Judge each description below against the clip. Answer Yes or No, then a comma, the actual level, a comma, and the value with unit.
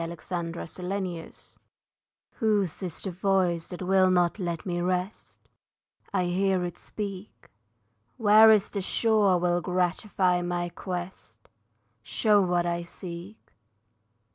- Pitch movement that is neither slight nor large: No, narrow, 2.0 semitones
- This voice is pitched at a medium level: Yes, medium, 180 Hz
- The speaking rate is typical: No, slow, 115 wpm